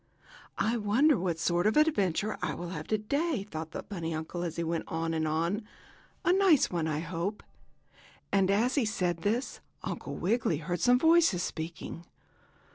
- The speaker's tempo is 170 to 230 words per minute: Yes, average, 175 wpm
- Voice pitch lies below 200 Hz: Yes, medium, 185 Hz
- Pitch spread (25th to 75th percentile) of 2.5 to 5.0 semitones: No, wide, 5.6 semitones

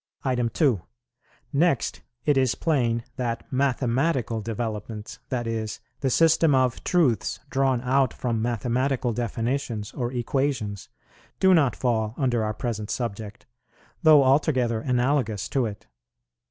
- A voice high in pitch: No, low, 125 Hz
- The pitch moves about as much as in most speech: Yes, average, 3.2 semitones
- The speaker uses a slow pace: Yes, slow, 120 wpm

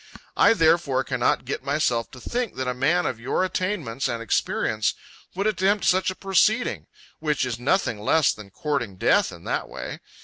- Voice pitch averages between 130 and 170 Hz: Yes, medium, 140 Hz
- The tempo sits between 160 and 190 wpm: Yes, average, 175 wpm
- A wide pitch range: Yes, wide, 7.3 semitones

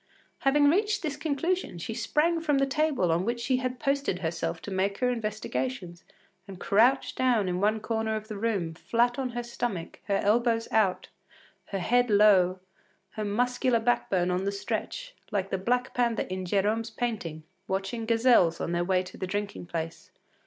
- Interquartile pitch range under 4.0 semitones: No, average, 4.8 semitones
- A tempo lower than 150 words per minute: No, average, 180 wpm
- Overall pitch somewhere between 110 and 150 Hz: No, high, 220 Hz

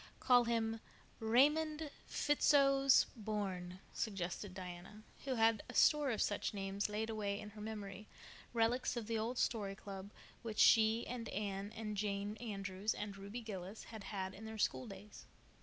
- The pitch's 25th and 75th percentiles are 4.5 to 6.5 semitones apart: No, narrow, 2.6 semitones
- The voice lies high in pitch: Yes, high, 215 Hz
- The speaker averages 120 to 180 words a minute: Yes, average, 150 wpm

